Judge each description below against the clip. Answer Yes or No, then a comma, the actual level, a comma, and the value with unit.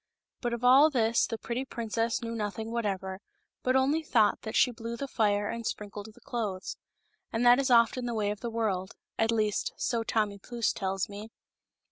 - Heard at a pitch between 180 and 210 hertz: No, high, 225 Hz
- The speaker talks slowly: No, average, 195 wpm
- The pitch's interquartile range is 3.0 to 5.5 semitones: No, narrow, 2.4 semitones